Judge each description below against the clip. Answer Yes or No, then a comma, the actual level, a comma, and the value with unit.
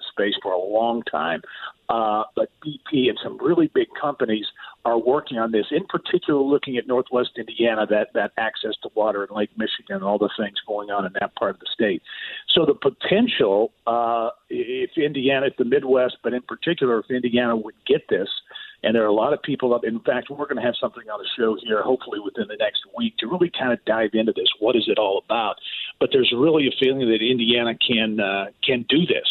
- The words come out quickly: Yes, fast, 220 wpm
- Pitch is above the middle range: No, low, 130 Hz